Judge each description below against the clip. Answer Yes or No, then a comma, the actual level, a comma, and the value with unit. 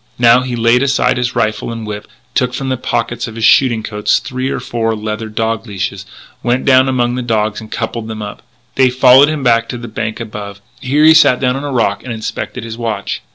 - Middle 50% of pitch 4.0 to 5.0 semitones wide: No, narrow, 2.6 semitones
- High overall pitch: No, low, 120 Hz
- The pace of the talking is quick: Yes, fast, 225 wpm